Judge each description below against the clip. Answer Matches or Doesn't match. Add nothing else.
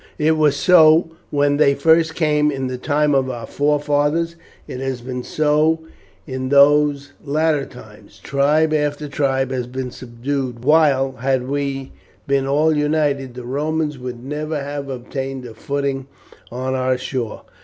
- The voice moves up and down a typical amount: Doesn't match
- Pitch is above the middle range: Doesn't match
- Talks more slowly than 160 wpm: Matches